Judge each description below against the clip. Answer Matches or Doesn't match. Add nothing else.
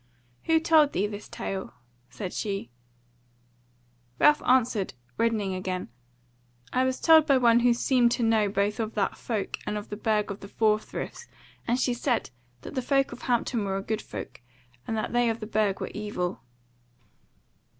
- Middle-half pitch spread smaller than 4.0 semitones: Matches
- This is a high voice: Matches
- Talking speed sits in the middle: Matches